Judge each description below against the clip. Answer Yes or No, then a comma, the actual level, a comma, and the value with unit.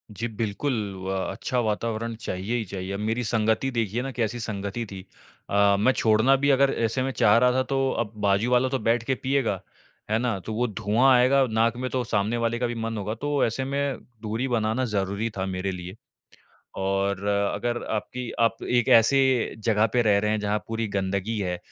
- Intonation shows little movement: No, average, 3.3 semitones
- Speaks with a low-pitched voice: Yes, low, 115 Hz